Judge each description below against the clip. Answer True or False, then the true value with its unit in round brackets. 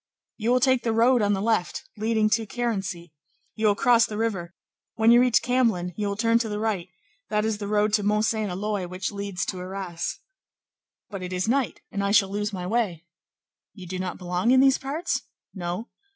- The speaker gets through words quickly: True (210 wpm)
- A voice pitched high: True (210 Hz)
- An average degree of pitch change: True (3.5 semitones)